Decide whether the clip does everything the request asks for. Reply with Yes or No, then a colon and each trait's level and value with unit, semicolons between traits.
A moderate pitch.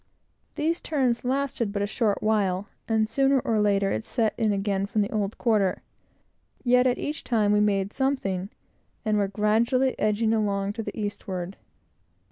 No: high, 215 Hz